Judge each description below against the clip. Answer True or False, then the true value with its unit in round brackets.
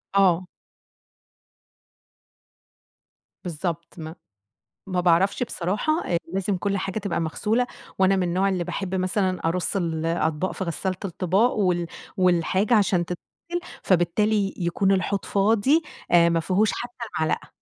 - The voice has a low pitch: False (185 Hz)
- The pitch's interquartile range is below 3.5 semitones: True (2.7 semitones)